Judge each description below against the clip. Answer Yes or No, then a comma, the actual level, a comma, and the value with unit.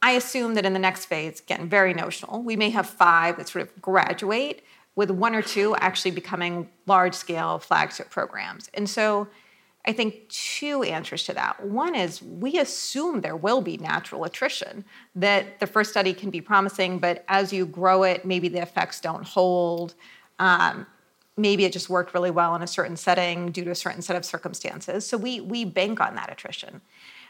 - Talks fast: No, average, 190 wpm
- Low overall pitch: No, high, 190 Hz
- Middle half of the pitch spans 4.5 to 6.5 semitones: No, average, 2.8 semitones